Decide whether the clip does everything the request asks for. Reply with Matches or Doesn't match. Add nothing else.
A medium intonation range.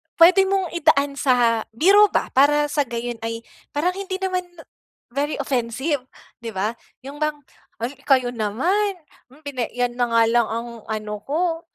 Doesn't match